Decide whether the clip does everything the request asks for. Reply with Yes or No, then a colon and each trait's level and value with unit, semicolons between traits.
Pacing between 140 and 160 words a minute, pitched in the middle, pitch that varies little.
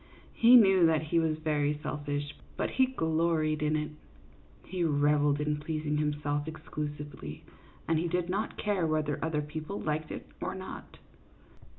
Yes: average, 155 wpm; medium, 155 Hz; narrow, 1.8 semitones